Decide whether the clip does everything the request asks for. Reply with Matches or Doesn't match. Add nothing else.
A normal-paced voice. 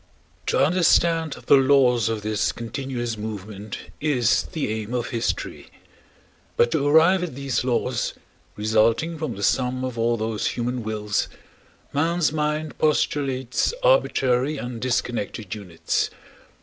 Doesn't match